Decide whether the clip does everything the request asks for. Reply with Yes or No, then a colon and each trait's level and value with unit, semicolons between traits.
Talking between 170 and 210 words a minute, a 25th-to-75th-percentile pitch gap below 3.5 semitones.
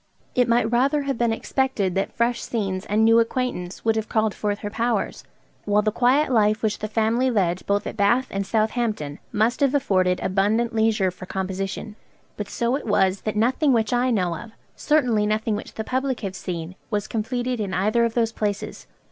Yes: average, 195 wpm; average, 3.1 semitones